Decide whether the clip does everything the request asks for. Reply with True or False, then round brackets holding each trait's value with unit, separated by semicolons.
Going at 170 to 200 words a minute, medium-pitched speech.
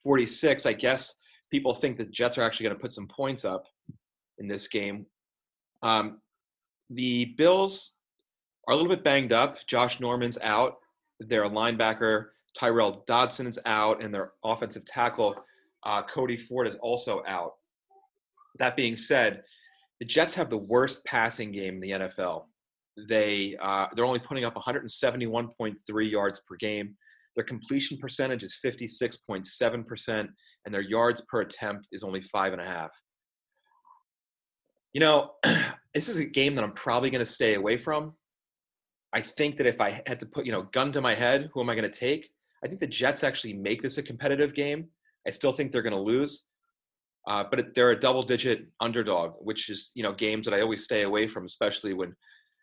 False (180 wpm; 120 Hz)